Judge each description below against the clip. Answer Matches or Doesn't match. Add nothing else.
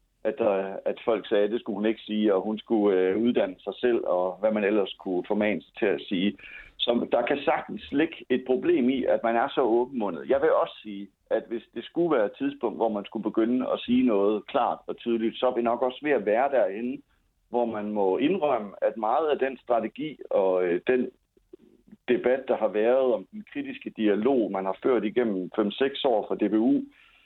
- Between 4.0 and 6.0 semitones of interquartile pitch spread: Matches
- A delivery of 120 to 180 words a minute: Doesn't match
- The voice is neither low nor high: Doesn't match